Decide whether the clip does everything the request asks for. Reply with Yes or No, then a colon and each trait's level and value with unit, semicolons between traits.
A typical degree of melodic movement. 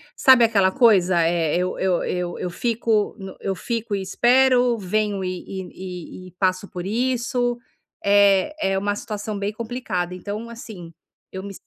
Yes: average, 4.0 semitones